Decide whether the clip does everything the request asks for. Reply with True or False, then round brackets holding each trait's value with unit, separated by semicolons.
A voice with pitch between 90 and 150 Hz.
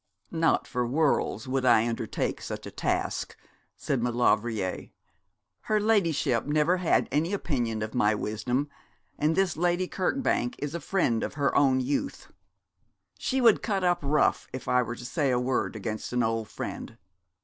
True (135 Hz)